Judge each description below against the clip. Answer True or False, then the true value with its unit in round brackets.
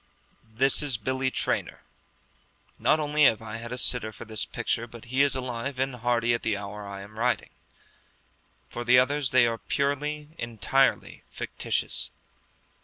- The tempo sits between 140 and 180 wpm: True (160 wpm)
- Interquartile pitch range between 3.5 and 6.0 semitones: False (3.1 semitones)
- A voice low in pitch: True (125 Hz)